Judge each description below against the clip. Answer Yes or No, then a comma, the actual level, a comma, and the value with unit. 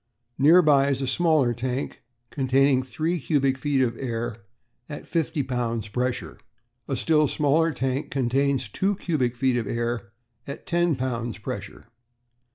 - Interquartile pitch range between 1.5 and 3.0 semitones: No, average, 3.5 semitones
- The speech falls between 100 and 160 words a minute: Yes, average, 155 wpm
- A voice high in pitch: No, low, 130 Hz